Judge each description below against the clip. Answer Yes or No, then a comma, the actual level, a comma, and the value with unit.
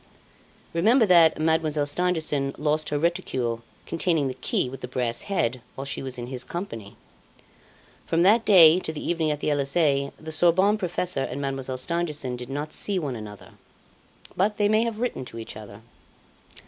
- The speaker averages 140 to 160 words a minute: No, average, 175 wpm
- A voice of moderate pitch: Yes, medium, 150 Hz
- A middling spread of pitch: Yes, average, 5.0 semitones